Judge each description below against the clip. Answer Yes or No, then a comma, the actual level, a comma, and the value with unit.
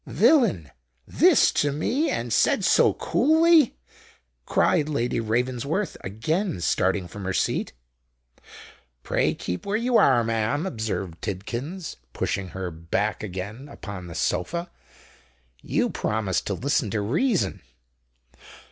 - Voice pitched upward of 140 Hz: No, low, 115 Hz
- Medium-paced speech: No, slow, 115 wpm